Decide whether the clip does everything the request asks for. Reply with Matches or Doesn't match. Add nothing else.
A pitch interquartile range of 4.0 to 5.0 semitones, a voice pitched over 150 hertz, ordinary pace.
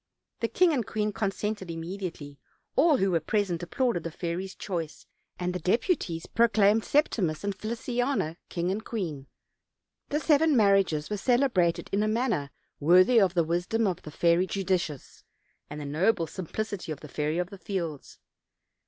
Matches